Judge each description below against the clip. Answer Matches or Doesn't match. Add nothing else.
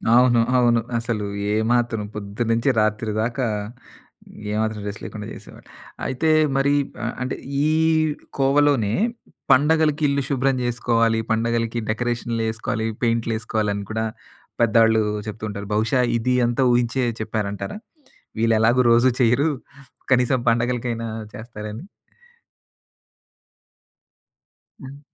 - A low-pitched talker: Matches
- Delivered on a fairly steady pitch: Matches